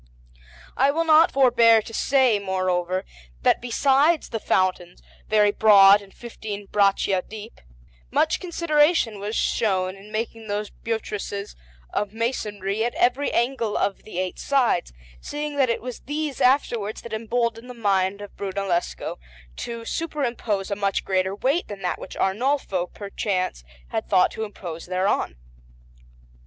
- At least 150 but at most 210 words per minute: No, average, 140 wpm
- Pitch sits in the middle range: No, high, 215 Hz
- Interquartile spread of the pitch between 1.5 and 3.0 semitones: No, average, 4.0 semitones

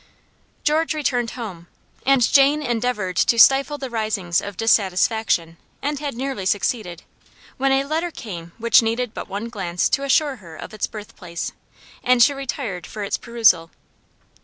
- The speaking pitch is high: Yes, high, 230 Hz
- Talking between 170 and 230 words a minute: No, average, 155 wpm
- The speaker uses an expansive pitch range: Yes, wide, 5.8 semitones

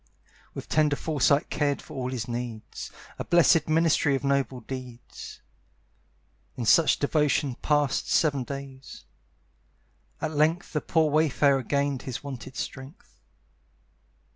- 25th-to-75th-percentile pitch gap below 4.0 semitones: Yes, average, 2.7 semitones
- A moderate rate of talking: No, slow, 120 wpm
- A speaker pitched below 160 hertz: Yes, medium, 140 Hz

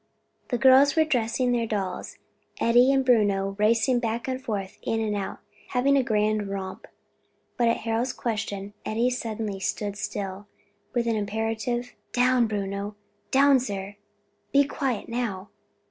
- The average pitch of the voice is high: Yes, high, 225 Hz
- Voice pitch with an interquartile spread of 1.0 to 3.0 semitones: No, average, 3.4 semitones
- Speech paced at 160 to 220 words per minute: No, average, 145 wpm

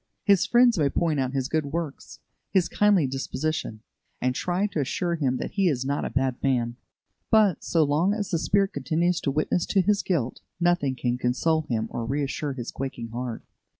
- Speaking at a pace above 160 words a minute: Yes, average, 190 wpm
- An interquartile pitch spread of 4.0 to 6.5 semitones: Yes, average, 5.2 semitones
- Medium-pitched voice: Yes, medium, 150 Hz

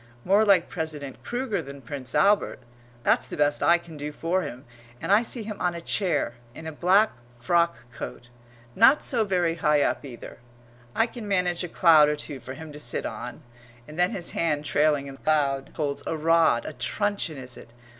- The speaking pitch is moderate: Yes, medium, 160 Hz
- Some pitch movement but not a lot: Yes, average, 4.5 semitones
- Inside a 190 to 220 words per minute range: Yes, average, 200 wpm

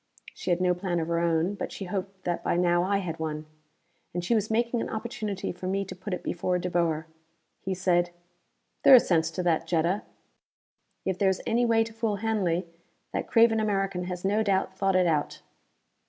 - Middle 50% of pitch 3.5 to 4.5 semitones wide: No, average, 2.9 semitones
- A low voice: No, medium, 185 Hz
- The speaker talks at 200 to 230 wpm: Yes, fast, 205 wpm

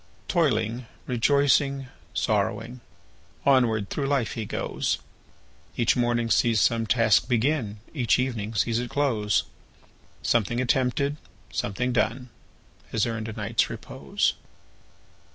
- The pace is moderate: No, slow, 100 wpm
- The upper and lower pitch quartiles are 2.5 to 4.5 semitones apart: Yes, average, 2.8 semitones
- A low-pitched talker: Yes, low, 120 Hz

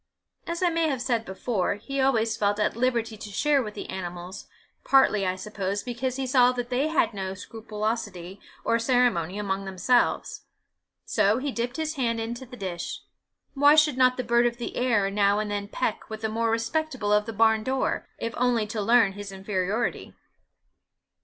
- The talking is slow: No, average, 180 wpm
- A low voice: No, high, 225 Hz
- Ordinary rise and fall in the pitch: Yes, average, 3.7 semitones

